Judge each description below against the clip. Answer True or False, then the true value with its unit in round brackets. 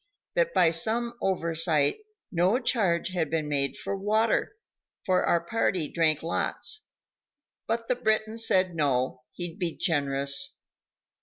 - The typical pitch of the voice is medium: True (175 Hz)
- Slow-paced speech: True (130 wpm)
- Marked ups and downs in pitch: True (5.7 semitones)